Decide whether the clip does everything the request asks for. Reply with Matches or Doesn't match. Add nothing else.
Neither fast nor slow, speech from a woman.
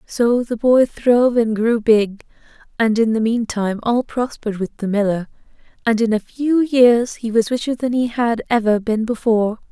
Matches